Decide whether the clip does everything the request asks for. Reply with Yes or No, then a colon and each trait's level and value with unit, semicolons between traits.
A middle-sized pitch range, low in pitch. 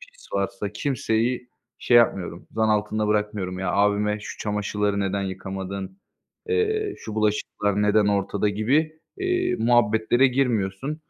Yes: average, 3.4 semitones; low, 105 Hz